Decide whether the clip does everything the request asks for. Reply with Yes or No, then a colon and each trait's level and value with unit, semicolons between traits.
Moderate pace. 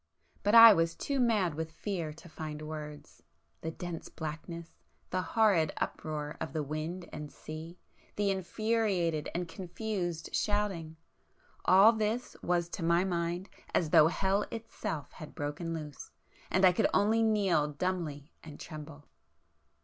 No: slow, 130 wpm